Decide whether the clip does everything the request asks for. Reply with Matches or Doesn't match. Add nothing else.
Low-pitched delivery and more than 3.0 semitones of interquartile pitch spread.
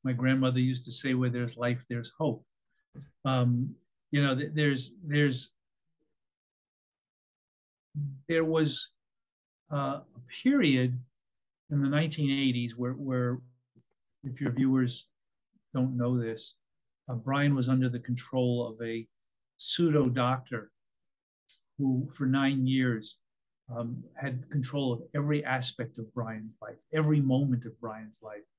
Doesn't match